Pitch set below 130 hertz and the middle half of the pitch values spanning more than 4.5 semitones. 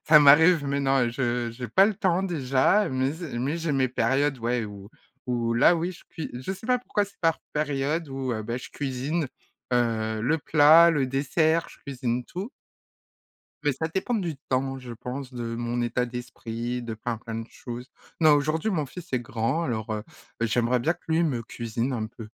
No: low, 135 Hz; average, 5.0 semitones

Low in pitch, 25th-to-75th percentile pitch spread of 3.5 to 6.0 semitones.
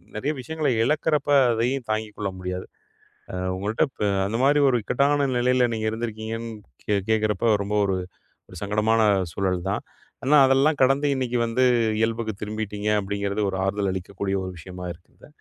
Yes: low, 110 Hz; average, 4.1 semitones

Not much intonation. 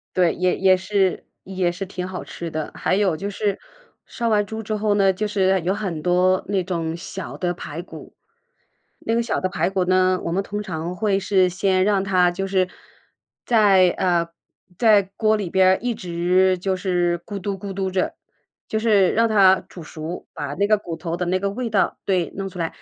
Yes: narrow, 2.2 semitones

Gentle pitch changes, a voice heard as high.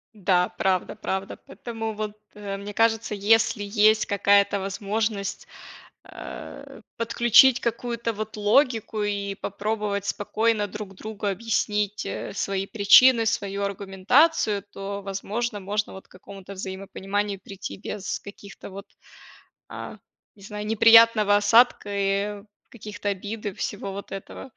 Yes: narrow, 1.9 semitones; high, 205 Hz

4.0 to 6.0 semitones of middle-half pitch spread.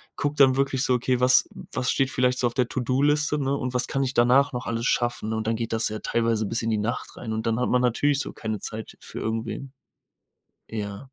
No: average, 2.8 semitones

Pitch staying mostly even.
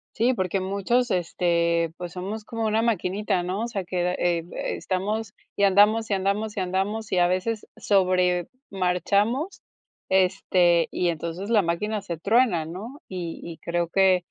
No: average, 3.1 semitones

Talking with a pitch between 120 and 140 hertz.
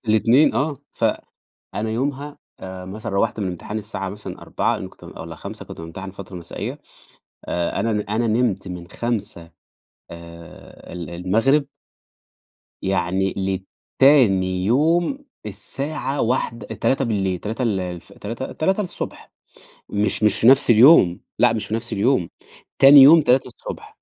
No: low, 110 Hz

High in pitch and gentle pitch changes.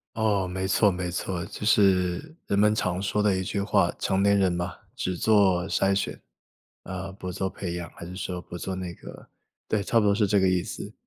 No: very low, 95 Hz; narrow, 2.0 semitones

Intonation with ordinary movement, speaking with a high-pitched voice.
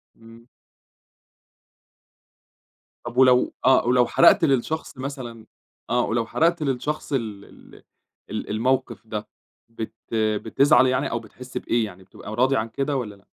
No: average, 3.3 semitones; low, 120 Hz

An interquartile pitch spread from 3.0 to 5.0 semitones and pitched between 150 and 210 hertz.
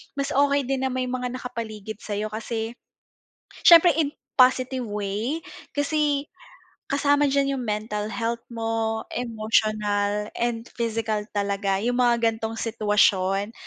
No: average, 3.6 semitones; high, 230 Hz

